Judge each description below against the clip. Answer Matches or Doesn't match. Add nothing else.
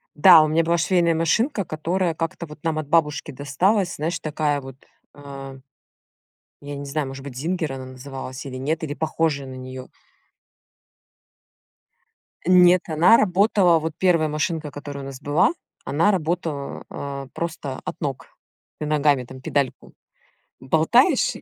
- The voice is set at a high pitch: Doesn't match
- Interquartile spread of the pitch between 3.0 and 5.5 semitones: Matches